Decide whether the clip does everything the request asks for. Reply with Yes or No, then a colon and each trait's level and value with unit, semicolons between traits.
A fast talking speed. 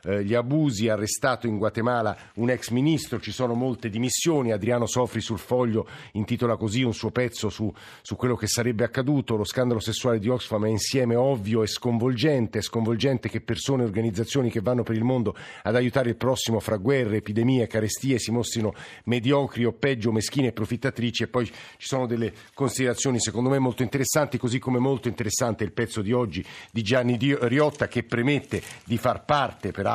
Yes: fast, 180 wpm